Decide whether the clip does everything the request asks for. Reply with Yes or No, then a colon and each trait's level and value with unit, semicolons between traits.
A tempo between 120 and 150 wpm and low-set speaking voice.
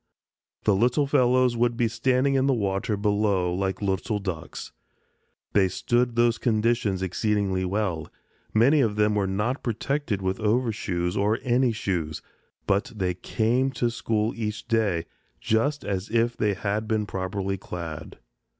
Yes: average, 145 wpm; low, 105 Hz